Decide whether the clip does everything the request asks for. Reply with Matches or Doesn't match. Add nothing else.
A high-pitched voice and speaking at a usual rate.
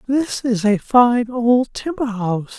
Matches